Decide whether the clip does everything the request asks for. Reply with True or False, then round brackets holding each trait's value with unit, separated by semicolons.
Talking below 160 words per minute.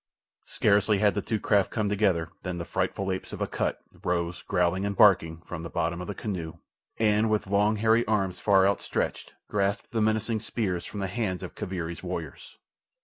False (185 wpm)